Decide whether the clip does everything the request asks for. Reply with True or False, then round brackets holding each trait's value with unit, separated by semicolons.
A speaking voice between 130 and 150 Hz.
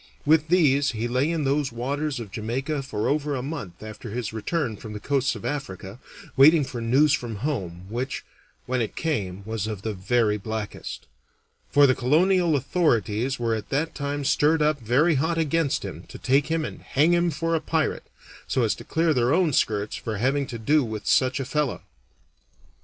True (135 Hz)